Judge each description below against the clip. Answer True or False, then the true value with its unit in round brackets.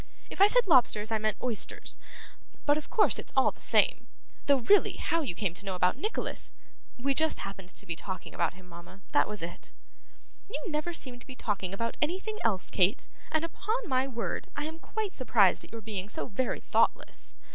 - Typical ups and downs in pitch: False (8.2 semitones)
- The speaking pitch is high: True (240 Hz)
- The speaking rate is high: True (210 wpm)